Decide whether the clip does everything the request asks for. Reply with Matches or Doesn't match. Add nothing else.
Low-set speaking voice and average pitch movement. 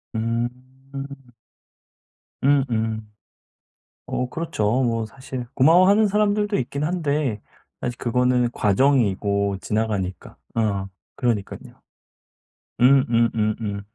Matches